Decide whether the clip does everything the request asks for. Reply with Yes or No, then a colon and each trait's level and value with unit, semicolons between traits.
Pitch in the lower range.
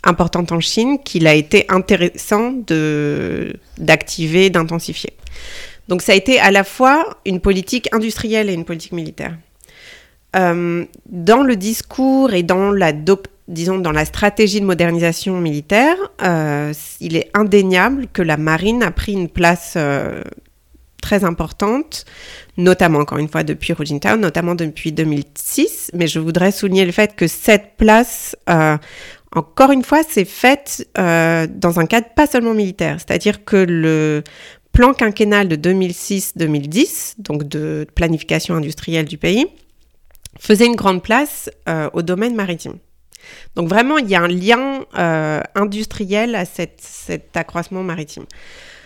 No: medium, 185 Hz